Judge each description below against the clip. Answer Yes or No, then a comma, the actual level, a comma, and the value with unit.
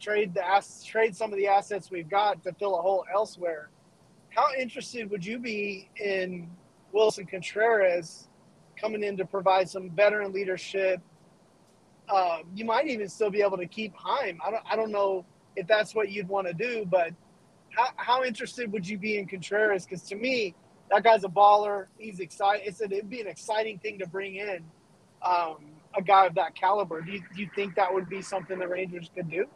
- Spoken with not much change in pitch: Yes, narrow, 2.3 semitones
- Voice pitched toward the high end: Yes, high, 195 Hz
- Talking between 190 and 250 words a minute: Yes, average, 195 wpm